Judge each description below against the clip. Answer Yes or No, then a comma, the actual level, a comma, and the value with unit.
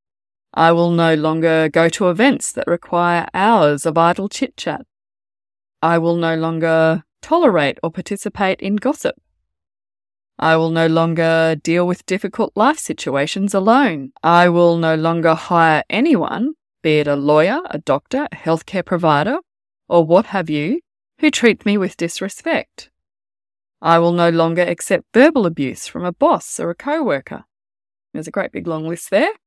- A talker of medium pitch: Yes, medium, 170 Hz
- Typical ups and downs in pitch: Yes, average, 4.0 semitones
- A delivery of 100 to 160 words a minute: Yes, average, 155 wpm